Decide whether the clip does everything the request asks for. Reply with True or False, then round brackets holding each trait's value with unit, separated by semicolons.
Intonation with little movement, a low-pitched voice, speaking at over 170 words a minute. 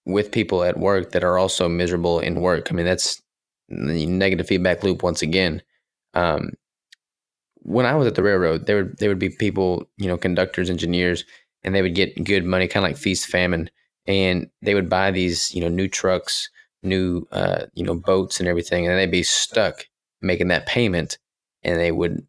True (1.6 semitones; 90 Hz; 195 wpm)